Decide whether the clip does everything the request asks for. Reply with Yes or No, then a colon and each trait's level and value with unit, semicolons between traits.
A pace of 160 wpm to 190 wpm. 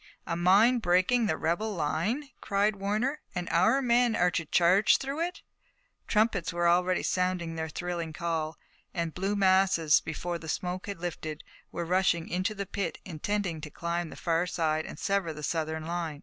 Yes: average, 175 wpm